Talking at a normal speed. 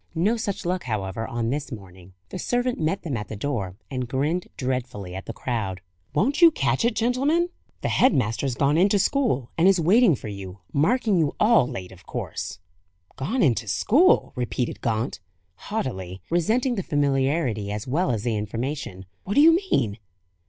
Yes: average, 175 wpm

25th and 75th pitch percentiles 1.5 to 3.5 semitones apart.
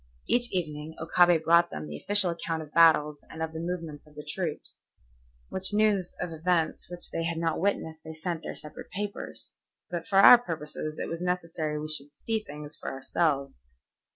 Yes: average, 2.7 semitones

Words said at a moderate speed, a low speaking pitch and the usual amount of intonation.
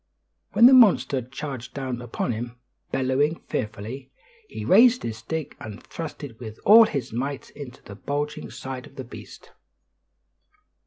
Yes: average, 150 wpm; low, 130 Hz; average, 3.9 semitones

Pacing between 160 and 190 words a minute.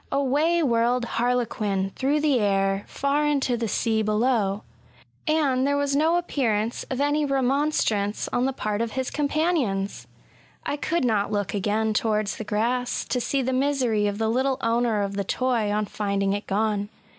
Yes: average, 170 wpm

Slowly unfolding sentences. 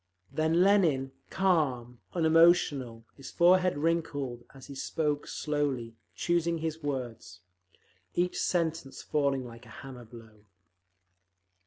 Yes: slow, 110 wpm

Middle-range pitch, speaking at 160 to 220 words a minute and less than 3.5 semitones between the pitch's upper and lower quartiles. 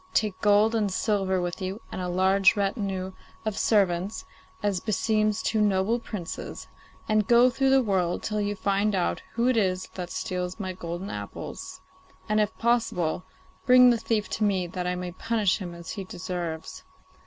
No: high, 195 Hz; average, 175 wpm; average, 2.9 semitones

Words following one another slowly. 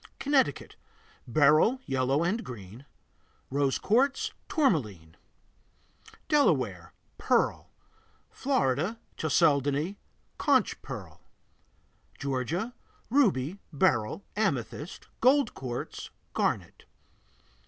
Yes: slow, 70 wpm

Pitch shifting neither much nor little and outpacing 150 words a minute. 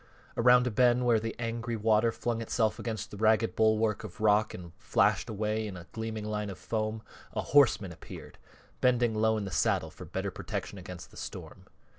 No: narrow, 1.4 semitones; average, 190 wpm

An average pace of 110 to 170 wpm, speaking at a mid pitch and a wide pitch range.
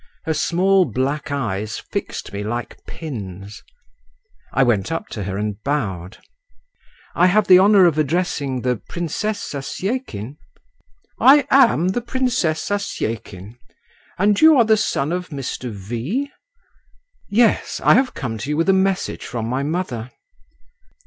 Yes: average, 140 wpm; medium, 150 Hz; wide, 9.0 semitones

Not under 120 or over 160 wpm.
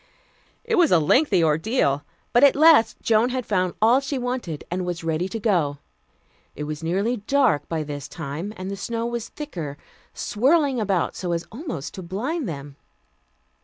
No: average, 170 wpm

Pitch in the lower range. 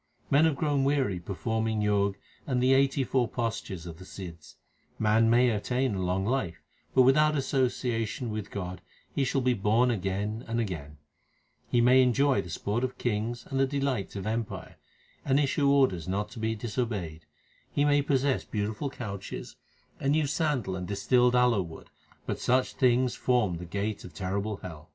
Yes: low, 115 Hz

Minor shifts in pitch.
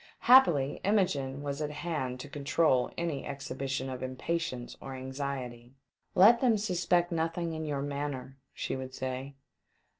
No: average, 4.2 semitones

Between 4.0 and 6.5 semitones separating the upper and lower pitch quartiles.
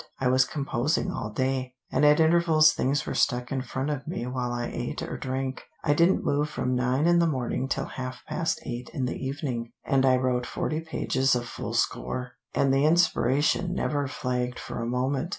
No: average, 2.9 semitones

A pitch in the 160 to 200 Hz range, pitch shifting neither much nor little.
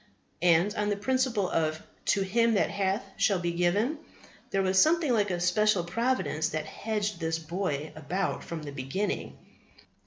Yes: high, 190 Hz; average, 4.0 semitones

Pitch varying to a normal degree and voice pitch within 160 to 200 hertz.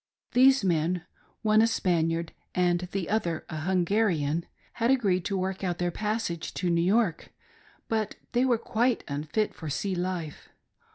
Yes: average, 4.4 semitones; medium, 185 Hz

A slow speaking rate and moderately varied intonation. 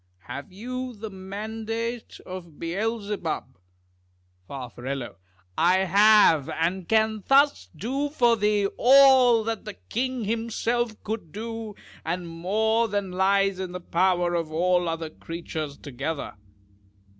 Yes: slow, 120 wpm; average, 4.7 semitones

